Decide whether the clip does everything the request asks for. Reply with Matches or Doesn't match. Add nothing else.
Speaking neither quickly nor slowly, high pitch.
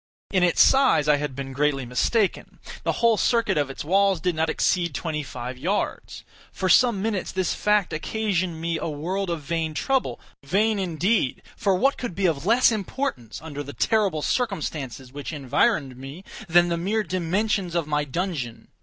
Doesn't match